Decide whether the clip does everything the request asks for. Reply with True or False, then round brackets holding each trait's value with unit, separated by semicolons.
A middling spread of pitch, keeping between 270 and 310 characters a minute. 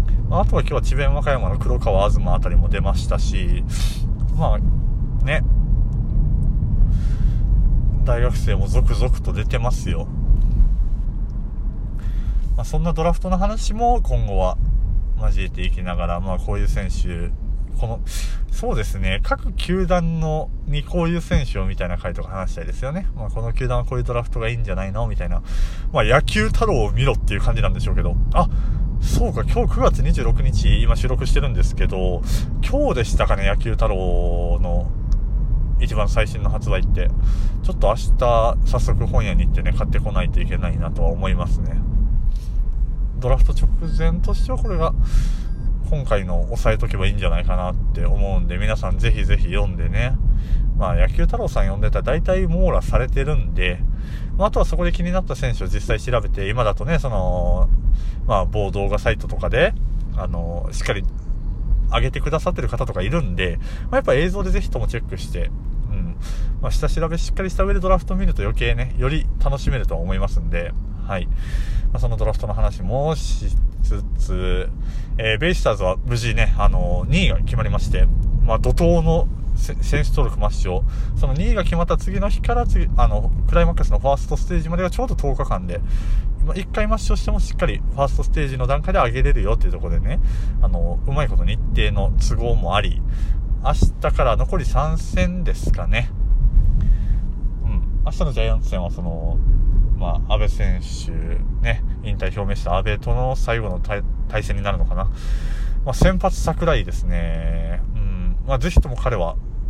False (4.9 semitones; 345 characters per minute)